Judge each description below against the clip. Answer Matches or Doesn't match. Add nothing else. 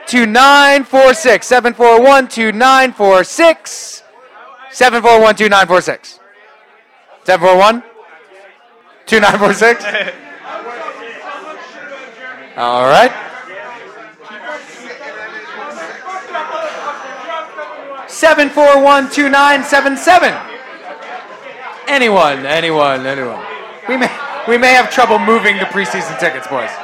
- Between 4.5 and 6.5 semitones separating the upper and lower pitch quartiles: Matches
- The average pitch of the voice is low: Doesn't match